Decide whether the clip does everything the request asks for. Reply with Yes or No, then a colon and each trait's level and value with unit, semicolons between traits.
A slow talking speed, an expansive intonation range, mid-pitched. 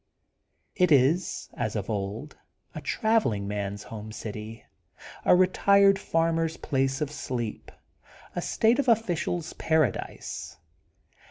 Yes: slow, 110 wpm; wide, 8.7 semitones; medium, 150 Hz